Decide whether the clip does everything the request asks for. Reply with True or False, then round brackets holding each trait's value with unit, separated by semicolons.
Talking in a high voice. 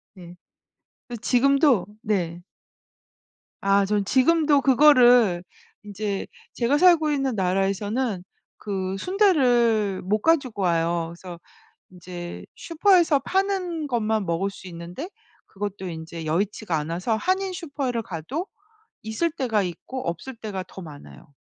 True (215 Hz)